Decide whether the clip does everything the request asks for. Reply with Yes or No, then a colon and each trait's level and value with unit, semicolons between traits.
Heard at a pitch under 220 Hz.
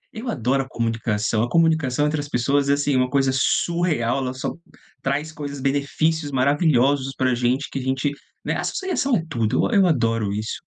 Yes: low, 135 Hz